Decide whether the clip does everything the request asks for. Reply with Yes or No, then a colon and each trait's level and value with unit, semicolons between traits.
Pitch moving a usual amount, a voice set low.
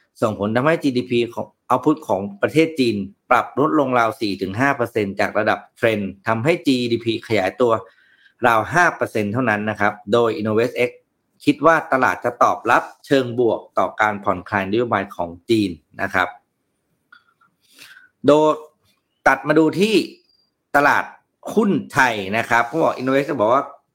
No: wide, 6.2 semitones; low, 120 Hz